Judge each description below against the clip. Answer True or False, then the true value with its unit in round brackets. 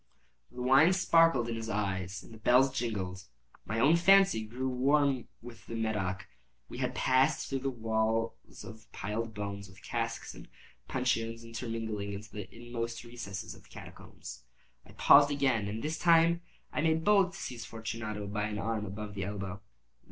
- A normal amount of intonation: True (4.0 semitones)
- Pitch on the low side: True (115 Hz)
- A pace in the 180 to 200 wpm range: False (165 wpm)